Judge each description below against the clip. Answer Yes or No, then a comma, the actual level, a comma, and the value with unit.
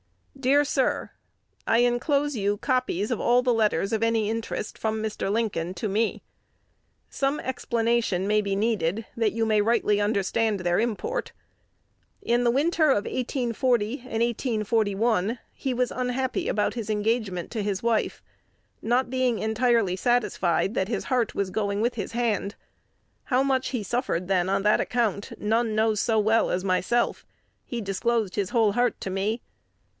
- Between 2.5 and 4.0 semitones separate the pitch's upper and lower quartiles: Yes, average, 3.0 semitones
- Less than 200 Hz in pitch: No, high, 225 Hz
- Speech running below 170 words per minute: Yes, average, 160 wpm